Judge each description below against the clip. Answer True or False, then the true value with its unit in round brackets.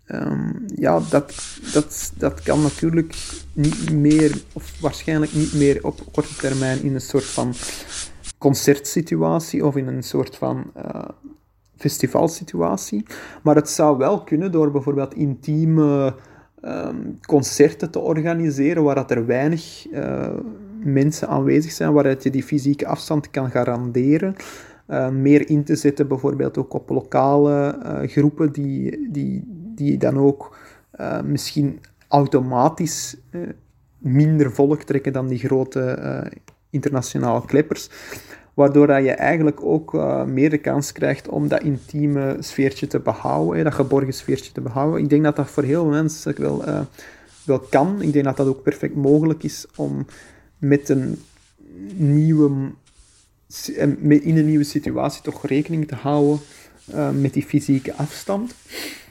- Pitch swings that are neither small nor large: False (2.2 semitones)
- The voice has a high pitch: False (145 Hz)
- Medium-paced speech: True (145 wpm)